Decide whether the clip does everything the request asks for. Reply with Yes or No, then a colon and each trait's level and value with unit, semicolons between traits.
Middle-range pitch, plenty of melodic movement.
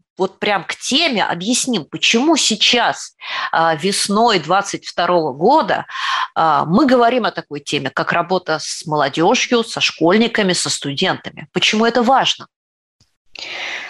No: high, 195 Hz; wide, 5.7 semitones